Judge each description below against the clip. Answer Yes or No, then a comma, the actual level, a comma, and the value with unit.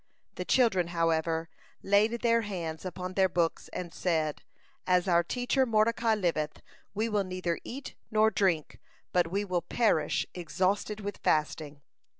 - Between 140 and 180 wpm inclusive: Yes, average, 145 wpm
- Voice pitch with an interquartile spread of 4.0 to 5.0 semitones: Yes, average, 4.3 semitones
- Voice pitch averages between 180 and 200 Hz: Yes, medium, 185 Hz